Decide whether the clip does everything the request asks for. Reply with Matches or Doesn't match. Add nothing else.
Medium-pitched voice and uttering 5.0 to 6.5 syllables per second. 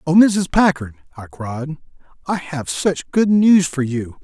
Doesn't match